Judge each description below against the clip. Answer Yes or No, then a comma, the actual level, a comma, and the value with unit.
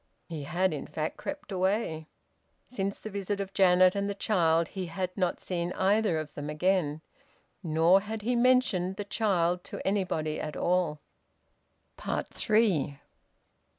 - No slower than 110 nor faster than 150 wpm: Yes, average, 145 wpm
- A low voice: No, medium, 185 Hz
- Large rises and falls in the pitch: No, average, 3.7 semitones